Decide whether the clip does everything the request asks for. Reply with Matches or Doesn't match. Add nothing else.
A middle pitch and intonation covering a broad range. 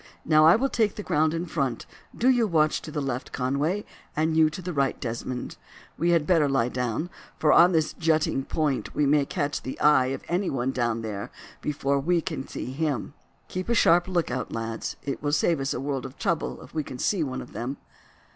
Doesn't match